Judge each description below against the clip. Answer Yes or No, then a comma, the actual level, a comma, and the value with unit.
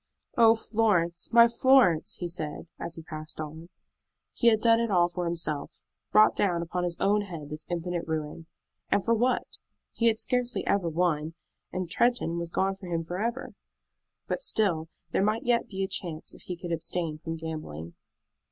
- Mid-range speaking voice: Yes, medium, 175 Hz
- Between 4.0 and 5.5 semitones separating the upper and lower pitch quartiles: Yes, average, 5.1 semitones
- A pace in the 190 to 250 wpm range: No, average, 180 wpm